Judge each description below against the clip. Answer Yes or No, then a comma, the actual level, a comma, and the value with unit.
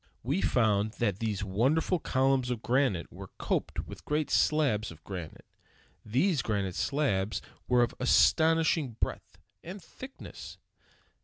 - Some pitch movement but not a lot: No, wide, 6.7 semitones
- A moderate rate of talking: No, slow, 130 wpm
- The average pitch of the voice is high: No, low, 120 Hz